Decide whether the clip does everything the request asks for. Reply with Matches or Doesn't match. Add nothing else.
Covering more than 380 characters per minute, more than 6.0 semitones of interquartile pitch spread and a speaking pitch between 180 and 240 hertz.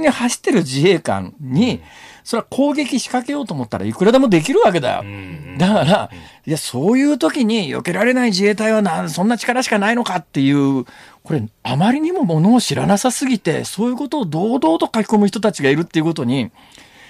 Matches